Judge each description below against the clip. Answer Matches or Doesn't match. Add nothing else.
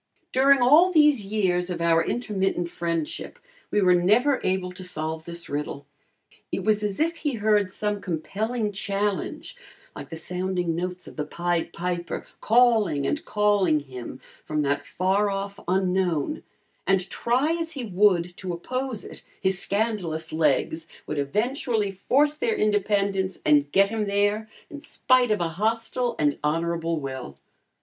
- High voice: Matches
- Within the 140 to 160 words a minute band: Matches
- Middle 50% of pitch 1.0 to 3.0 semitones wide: Doesn't match